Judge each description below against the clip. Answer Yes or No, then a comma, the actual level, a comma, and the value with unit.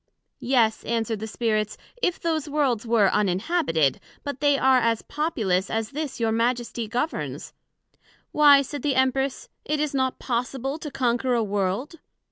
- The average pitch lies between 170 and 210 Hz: No, very high, 250 Hz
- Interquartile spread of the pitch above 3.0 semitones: Yes, average, 4.3 semitones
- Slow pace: No, average, 150 wpm